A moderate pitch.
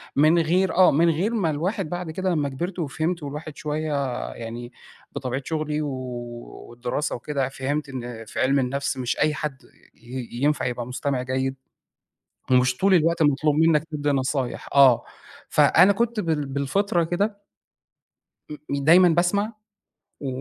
Yes: medium, 150 Hz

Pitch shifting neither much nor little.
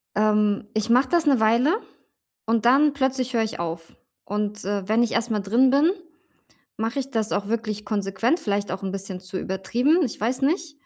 Yes: average, 4.2 semitones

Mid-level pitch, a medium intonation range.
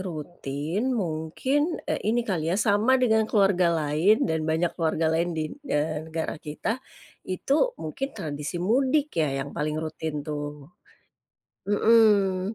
No: medium, 175 Hz; wide, 5.9 semitones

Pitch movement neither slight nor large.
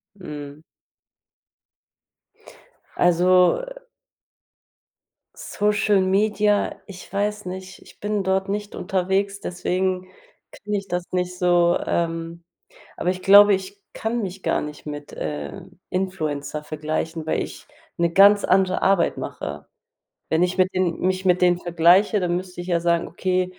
No: narrow, 2.3 semitones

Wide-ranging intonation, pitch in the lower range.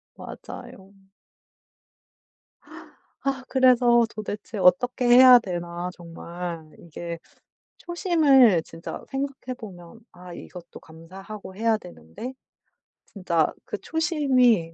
No: wide, 6.7 semitones; high, 210 Hz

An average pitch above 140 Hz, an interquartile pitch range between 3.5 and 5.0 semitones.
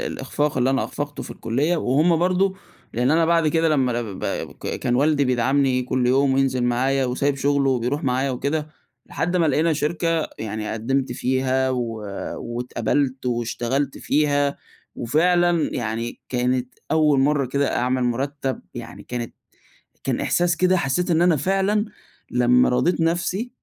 No: low, 135 Hz; average, 4.1 semitones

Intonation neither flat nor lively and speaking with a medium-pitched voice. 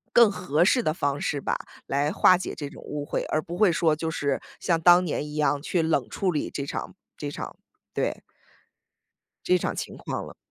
Yes: average, 3.5 semitones; medium, 155 Hz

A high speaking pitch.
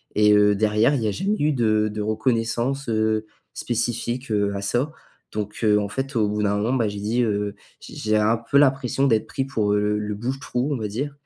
No: low, 110 Hz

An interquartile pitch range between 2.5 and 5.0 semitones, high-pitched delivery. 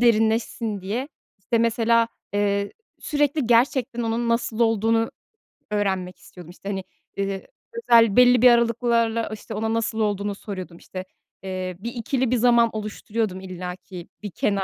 Yes: average, 2.9 semitones; high, 225 Hz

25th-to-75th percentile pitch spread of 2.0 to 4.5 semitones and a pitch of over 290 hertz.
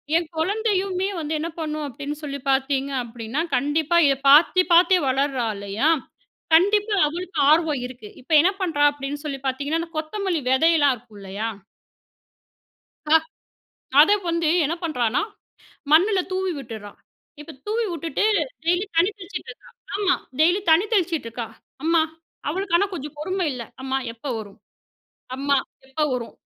No: average, 4.9 semitones; very high, 310 Hz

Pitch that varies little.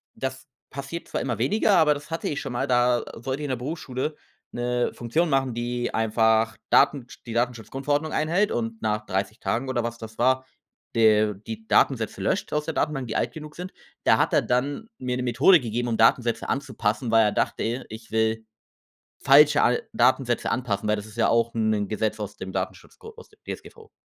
No: average, 3.8 semitones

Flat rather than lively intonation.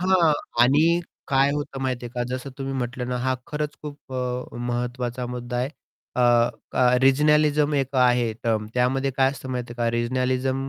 Yes: narrow, 2.2 semitones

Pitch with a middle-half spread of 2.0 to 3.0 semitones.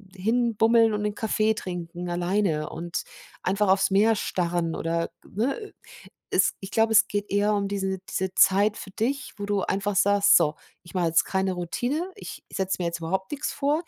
No: average, 3.5 semitones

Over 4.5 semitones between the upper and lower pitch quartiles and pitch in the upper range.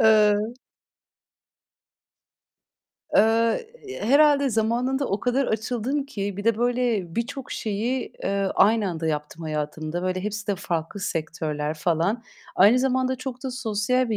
Yes: average, 5.3 semitones; high, 215 Hz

